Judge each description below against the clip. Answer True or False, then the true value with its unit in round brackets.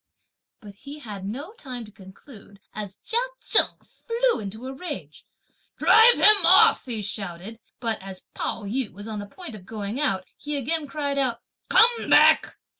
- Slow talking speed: False (170 wpm)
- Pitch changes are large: True (6.5 semitones)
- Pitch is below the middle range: False (230 Hz)